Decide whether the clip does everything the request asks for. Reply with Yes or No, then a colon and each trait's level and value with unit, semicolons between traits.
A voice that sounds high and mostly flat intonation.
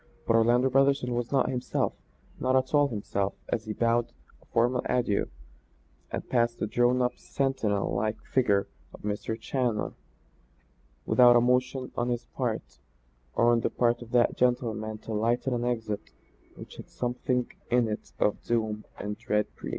No: low, 120 Hz; narrow, 2.3 semitones